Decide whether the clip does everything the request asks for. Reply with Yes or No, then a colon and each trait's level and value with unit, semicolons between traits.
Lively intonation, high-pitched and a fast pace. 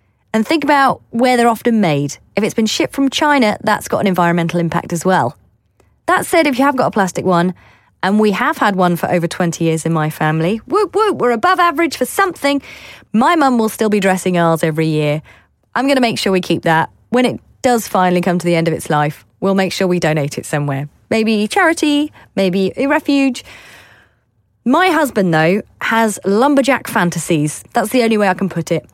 Yes: wide, 7.2 semitones; high, 195 Hz; fast, 210 wpm